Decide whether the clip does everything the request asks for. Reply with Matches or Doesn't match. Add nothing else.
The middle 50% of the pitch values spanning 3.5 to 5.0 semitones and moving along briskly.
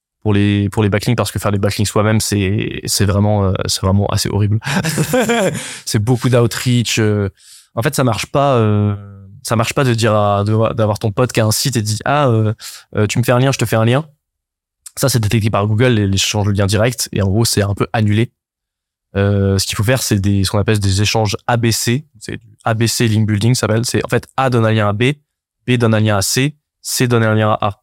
Doesn't match